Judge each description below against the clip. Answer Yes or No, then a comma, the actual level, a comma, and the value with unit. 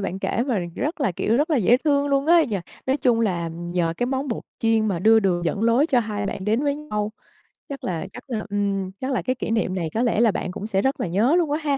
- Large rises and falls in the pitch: Yes, wide, 5.7 semitones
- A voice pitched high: Yes, high, 225 Hz